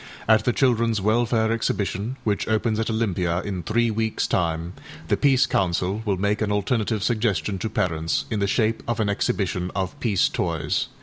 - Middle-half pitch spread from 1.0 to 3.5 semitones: Yes, average, 3.0 semitones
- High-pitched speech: No, low, 105 Hz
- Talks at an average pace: Yes, average, 175 wpm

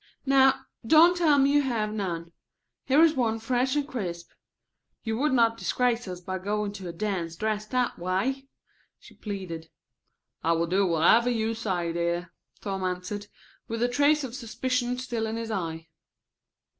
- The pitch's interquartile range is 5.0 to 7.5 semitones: Yes, wide, 5.6 semitones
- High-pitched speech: Yes, high, 220 Hz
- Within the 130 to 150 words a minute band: No, average, 165 wpm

